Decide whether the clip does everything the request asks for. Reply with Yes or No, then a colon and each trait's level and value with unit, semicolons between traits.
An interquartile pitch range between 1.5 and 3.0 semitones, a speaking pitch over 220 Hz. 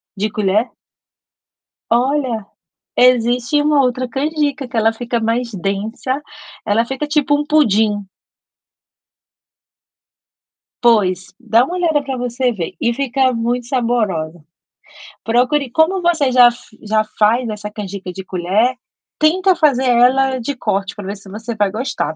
No: average, 4.0 semitones; high, 240 Hz